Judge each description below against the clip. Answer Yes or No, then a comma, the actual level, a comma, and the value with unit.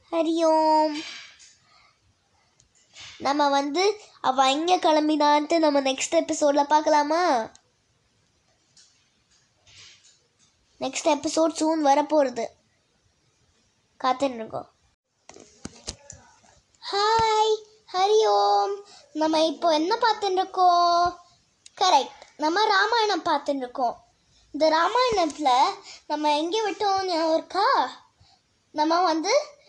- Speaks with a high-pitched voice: Yes, very high, 320 Hz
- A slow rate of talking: Yes, slow, 70 wpm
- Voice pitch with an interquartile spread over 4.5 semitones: No, average, 4.2 semitones